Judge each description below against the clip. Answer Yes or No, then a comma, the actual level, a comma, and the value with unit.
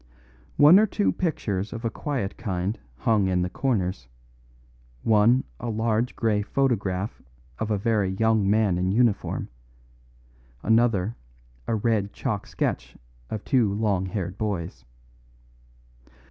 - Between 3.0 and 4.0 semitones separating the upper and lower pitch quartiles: Yes, average, 3.3 semitones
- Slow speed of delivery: Yes, slow, 125 wpm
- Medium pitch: No, low, 105 Hz